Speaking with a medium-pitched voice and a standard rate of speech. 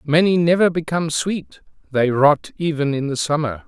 Yes: medium, 150 Hz; average, 165 wpm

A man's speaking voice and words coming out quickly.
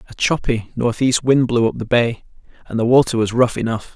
Yes: male; fast, 210 wpm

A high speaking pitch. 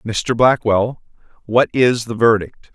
No: low, 115 Hz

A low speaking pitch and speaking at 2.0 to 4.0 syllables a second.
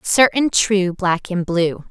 No: high, 190 Hz; 3.3 syllables/s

